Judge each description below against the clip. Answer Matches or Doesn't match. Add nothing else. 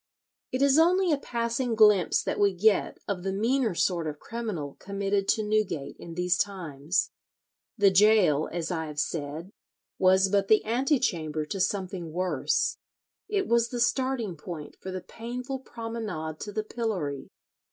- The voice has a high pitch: Matches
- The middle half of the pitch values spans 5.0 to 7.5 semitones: Matches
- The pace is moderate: Matches